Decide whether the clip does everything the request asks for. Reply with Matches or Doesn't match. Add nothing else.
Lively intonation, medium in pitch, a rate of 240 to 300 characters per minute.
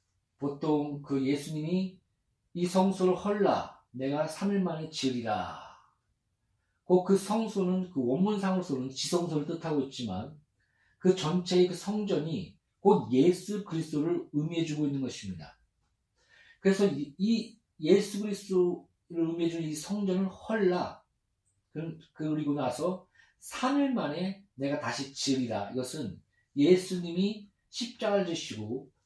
Matches